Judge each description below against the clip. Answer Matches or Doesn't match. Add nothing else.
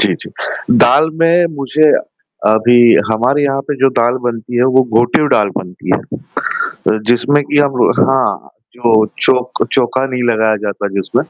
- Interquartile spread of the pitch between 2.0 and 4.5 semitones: Matches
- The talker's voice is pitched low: Matches